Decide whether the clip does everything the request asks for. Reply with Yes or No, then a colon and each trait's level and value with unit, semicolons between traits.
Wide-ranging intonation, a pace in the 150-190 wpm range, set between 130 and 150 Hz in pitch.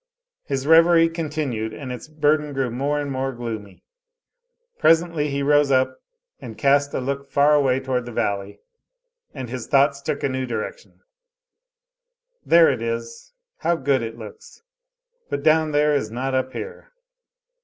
No: average, 3.1 semitones; average, 155 wpm; medium, 140 Hz